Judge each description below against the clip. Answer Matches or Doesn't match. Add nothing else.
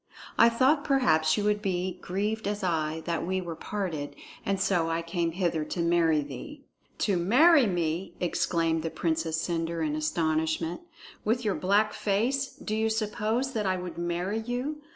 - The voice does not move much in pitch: Doesn't match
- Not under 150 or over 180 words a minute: Matches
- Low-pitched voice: Doesn't match